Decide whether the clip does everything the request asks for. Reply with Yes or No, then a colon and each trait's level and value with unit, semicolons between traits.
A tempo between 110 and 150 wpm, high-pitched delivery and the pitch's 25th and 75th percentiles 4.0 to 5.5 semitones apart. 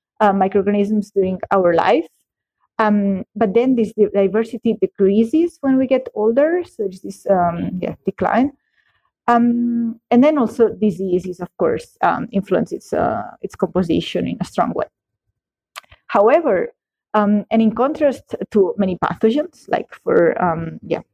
Yes: average, 140 wpm; high, 220 Hz; average, 4.5 semitones